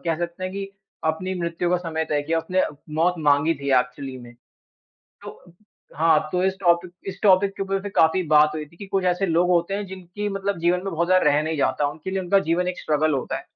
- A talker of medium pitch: Yes, medium, 175 Hz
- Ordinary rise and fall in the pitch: Yes, average, 3.1 semitones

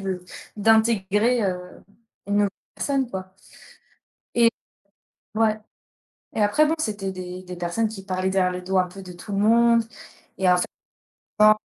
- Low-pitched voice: No, high, 200 Hz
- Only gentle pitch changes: No, average, 3.3 semitones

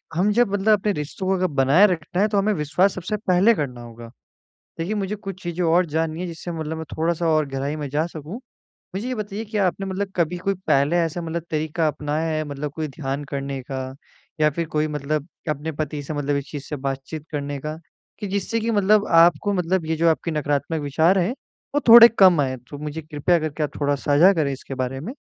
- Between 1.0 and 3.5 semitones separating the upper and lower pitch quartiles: No, average, 4.4 semitones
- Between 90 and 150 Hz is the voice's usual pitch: No, medium, 160 Hz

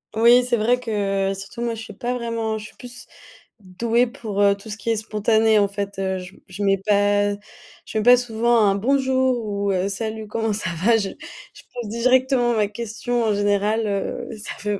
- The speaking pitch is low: No, high, 220 Hz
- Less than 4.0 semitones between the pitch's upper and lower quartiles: Yes, average, 2.7 semitones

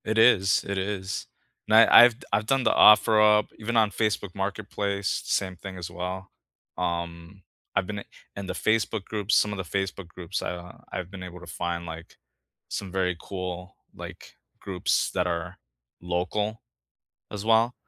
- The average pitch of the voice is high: No, very low, 95 Hz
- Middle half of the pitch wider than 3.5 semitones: No, average, 2.8 semitones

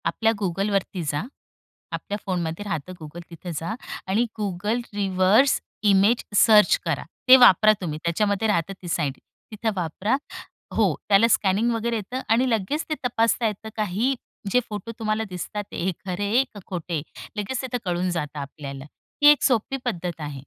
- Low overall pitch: No, high, 200 Hz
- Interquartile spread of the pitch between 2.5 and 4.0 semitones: No, average, 4.4 semitones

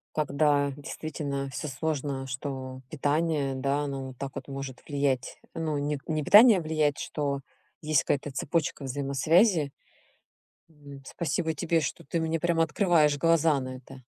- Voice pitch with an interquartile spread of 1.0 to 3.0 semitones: Yes, narrow, 2.5 semitones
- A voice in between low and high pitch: Yes, medium, 145 Hz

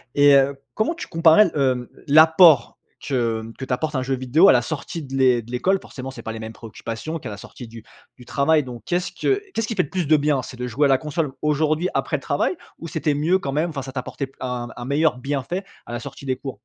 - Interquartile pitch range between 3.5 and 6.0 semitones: Yes, average, 4.2 semitones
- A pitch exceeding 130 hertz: Yes, medium, 140 Hz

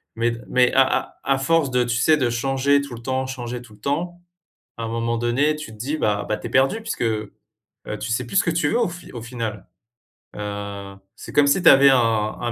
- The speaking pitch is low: Yes, low, 125 Hz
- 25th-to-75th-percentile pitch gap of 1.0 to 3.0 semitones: No, average, 3.7 semitones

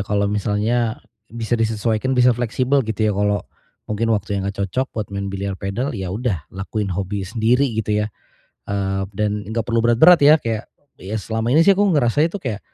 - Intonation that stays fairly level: No, average, 3.1 semitones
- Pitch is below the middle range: Yes, low, 110 Hz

